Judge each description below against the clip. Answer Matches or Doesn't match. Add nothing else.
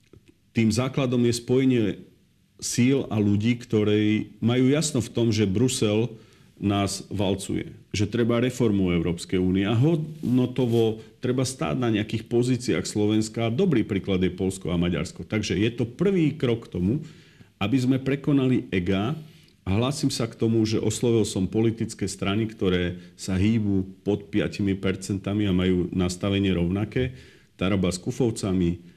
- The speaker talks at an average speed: Matches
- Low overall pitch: Matches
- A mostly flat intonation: Doesn't match